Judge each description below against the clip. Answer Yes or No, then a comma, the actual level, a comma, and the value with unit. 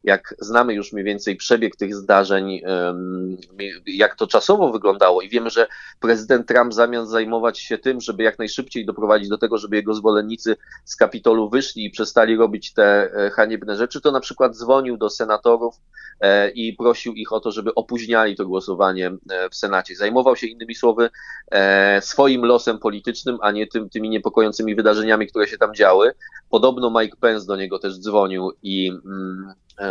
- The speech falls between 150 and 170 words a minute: Yes, fast, 160 wpm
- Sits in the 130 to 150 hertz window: No, low, 110 Hz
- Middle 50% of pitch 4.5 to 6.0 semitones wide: No, average, 2.8 semitones